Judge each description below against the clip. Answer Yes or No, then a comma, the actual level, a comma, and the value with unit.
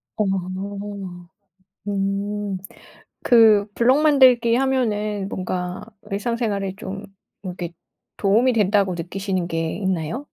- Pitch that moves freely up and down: No, average, 3.5 semitones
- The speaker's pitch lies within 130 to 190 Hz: No, high, 205 Hz